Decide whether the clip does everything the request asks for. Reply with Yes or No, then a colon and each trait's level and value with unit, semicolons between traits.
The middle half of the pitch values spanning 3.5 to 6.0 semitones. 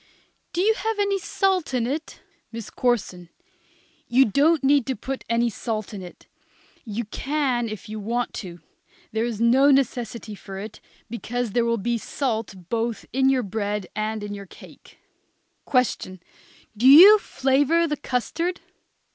Yes: average, 4.3 semitones